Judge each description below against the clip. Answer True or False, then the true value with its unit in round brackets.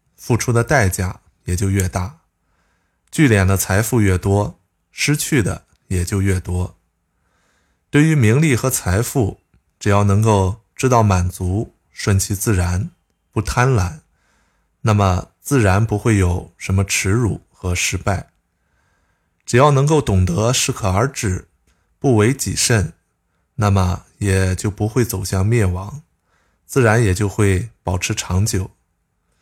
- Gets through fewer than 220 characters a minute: True (190 characters per minute)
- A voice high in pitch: False (95 Hz)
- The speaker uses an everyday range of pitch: True (3.9 semitones)